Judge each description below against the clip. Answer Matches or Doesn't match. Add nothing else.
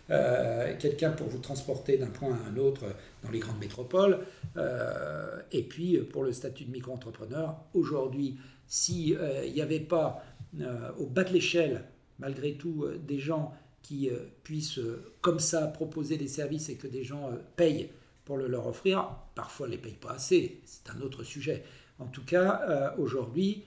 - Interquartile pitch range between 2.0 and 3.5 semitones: Doesn't match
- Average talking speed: Matches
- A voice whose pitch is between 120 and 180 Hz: Matches